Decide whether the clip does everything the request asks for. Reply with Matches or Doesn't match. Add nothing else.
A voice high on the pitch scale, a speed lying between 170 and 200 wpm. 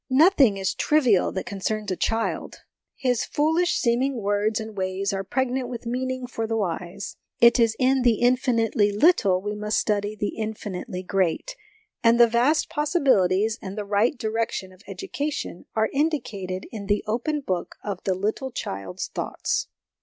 Doesn't match